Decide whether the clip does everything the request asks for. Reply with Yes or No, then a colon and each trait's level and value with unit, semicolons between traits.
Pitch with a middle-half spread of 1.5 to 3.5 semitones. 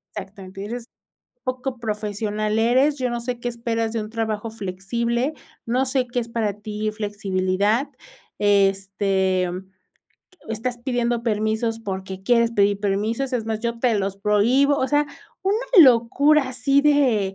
Yes: average, 3.2 semitones